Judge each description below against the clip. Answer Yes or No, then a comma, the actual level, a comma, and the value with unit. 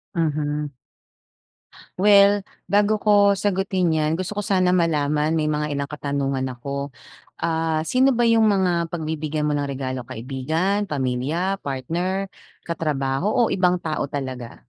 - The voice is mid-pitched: Yes, medium, 160 Hz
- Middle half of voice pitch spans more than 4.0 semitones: Yes, average, 5.1 semitones